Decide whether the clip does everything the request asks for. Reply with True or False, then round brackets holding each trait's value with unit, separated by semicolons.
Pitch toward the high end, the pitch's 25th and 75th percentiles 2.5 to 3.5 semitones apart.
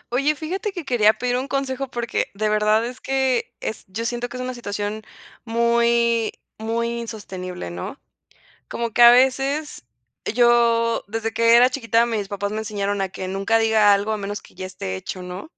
True (230 Hz; 3.0 semitones)